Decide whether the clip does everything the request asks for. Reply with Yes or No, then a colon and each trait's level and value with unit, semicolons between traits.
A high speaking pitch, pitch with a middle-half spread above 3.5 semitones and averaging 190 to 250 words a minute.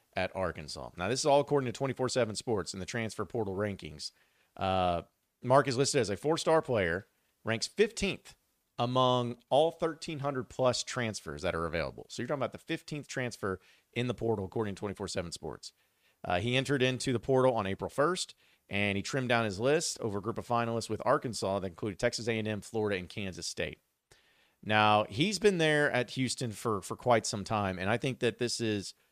No: low, 115 Hz; average, 4.5 semitones; fast, 205 wpm